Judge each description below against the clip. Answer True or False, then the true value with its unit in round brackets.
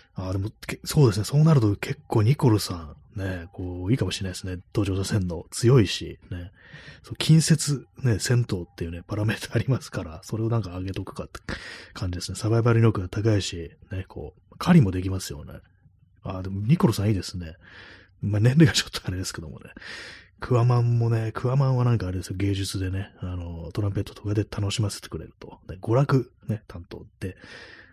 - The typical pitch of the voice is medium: False (100 Hz)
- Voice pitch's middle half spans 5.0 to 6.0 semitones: False (4.1 semitones)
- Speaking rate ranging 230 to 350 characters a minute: False (405 characters per minute)